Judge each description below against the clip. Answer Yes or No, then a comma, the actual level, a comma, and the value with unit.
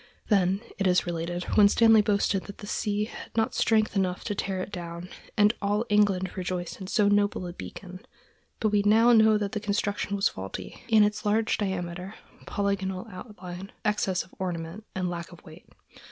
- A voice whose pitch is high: Yes, high, 200 Hz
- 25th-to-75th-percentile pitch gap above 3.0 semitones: No, narrow, 2.5 semitones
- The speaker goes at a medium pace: Yes, average, 180 wpm